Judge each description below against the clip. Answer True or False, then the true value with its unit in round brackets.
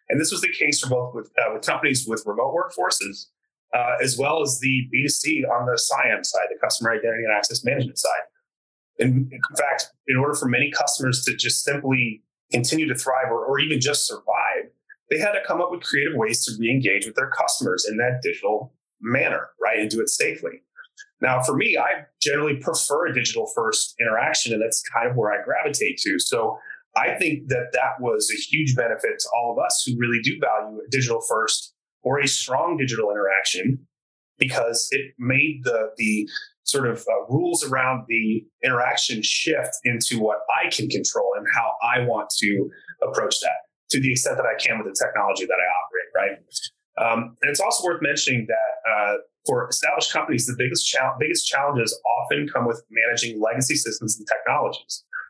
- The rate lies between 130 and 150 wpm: False (195 wpm)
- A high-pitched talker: False (135 Hz)